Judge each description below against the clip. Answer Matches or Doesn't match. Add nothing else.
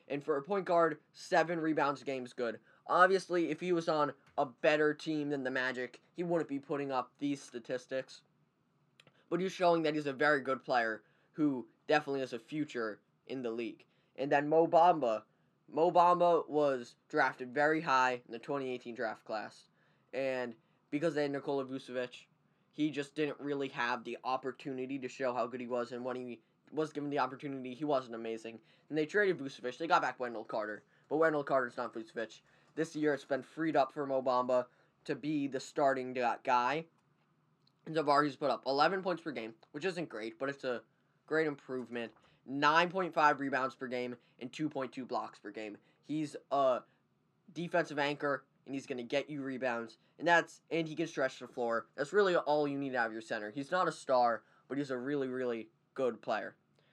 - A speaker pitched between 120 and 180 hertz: Matches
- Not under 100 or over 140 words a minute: Doesn't match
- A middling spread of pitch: Matches